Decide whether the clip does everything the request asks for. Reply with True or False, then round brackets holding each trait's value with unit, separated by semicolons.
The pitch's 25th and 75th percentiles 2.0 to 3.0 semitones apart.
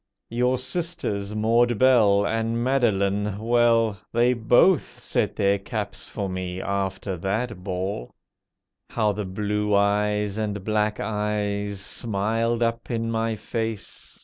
True (2.5 semitones)